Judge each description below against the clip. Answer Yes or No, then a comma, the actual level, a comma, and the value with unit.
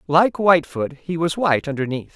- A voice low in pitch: No, medium, 160 Hz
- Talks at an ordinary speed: Yes, average, 165 wpm